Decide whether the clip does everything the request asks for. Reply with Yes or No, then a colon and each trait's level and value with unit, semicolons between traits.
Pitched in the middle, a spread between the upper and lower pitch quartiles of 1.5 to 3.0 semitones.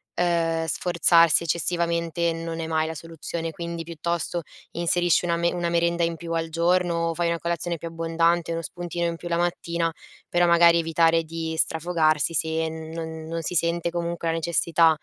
No: medium, 170 Hz; narrow, 0.7 semitones